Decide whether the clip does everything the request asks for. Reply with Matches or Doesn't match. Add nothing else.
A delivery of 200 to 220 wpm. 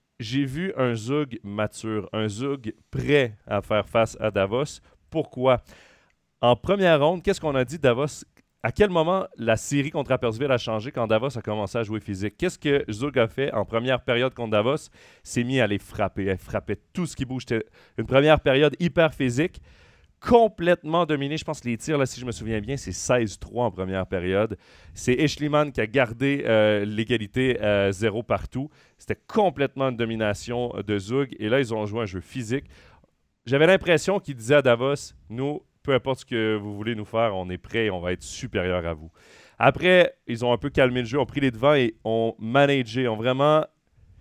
Matches